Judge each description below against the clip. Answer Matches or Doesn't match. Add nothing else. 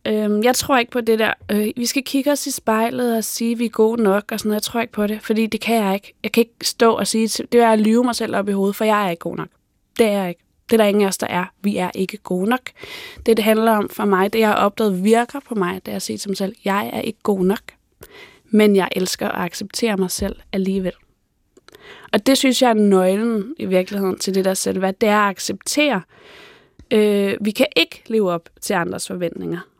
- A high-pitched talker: Matches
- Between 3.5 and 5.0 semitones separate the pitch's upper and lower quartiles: Doesn't match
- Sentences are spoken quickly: Matches